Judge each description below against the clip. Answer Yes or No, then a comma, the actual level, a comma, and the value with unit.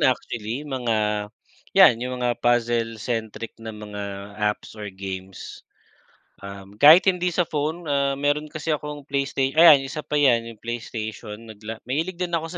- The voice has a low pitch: Yes, low, 120 Hz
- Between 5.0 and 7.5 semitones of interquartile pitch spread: Yes, average, 5.3 semitones